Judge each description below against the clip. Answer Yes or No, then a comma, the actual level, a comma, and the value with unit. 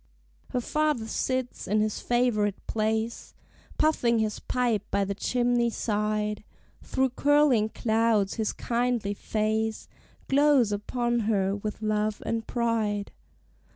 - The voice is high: Yes, high, 220 Hz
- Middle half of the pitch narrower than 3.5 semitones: Yes, narrow, 2.5 semitones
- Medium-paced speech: No, slow, 120 wpm